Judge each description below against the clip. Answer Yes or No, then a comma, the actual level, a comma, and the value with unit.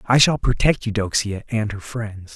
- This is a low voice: Yes, low, 110 Hz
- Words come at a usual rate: Yes, average, 180 wpm